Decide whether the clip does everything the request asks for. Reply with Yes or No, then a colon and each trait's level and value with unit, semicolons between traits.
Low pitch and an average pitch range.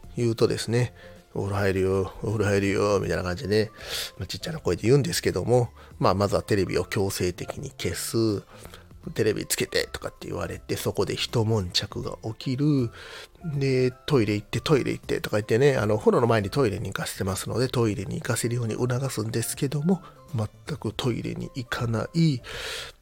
Yes: low, 110 Hz; average, 4.0 semitones